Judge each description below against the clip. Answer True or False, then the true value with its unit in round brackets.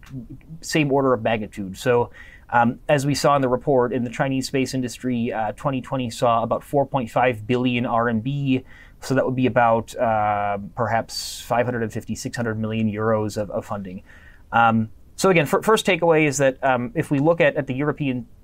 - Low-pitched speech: True (125 Hz)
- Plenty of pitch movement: False (3.6 semitones)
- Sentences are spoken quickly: False (175 wpm)